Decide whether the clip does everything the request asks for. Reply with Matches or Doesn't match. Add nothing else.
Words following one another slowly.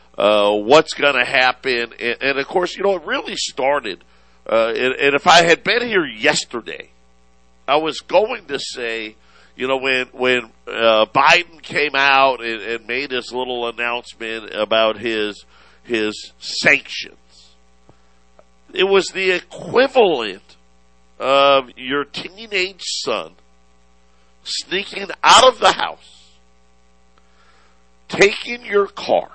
Matches